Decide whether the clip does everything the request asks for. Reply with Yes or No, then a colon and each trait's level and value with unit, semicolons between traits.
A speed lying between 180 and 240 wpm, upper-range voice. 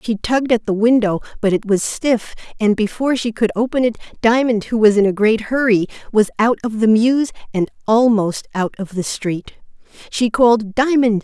Yes: average, 190 wpm; high, 225 Hz